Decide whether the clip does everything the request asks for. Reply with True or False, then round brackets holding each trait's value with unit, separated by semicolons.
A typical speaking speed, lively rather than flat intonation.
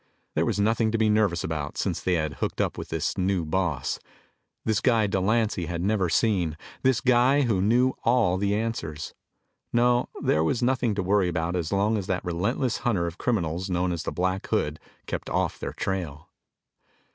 False (185 wpm; 4.7 semitones)